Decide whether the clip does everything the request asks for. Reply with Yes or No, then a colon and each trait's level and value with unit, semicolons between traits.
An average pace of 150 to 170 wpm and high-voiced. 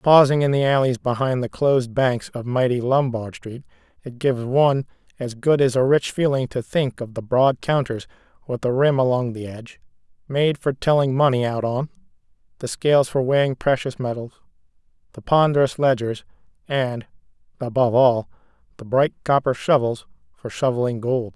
No: average, 165 wpm; low, 130 Hz